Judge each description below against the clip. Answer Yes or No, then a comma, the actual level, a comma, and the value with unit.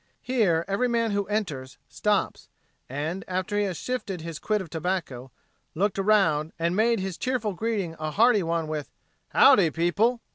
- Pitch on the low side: No, high, 190 Hz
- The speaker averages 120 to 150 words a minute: No, average, 160 wpm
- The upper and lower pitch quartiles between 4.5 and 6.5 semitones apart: Yes, average, 4.8 semitones